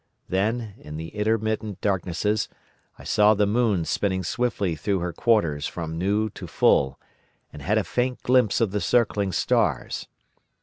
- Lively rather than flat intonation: No, average, 3.7 semitones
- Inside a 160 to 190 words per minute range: No, average, 150 wpm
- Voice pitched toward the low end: Yes, low, 105 Hz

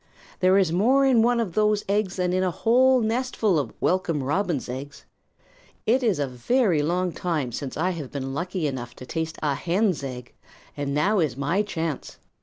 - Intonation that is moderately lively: No, wide, 6.6 semitones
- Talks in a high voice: No, medium, 175 Hz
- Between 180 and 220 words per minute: Yes, average, 190 wpm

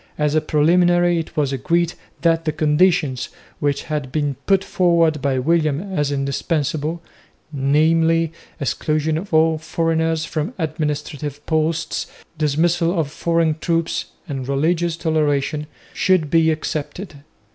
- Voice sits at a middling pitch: Yes, medium, 155 Hz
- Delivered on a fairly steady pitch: Yes, narrow, 2.1 semitones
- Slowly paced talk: Yes, slow, 125 wpm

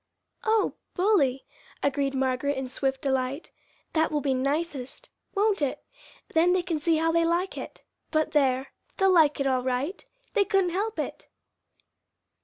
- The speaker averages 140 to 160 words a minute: Yes, average, 155 wpm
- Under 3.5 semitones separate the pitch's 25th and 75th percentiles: No, average, 5.0 semitones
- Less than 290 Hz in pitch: No, very high, 300 Hz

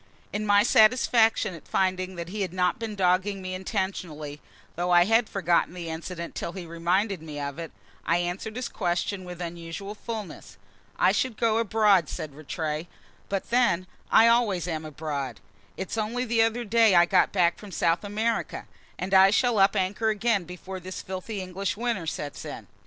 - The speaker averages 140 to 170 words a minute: No, average, 180 wpm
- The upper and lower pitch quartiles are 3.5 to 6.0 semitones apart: Yes, average, 3.9 semitones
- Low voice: No, high, 190 Hz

